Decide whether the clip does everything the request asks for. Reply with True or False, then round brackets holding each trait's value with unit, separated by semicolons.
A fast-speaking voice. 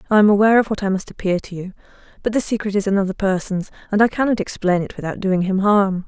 True (245 wpm)